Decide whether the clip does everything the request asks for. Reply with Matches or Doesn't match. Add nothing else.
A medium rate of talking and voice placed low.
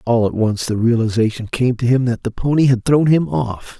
Doesn't match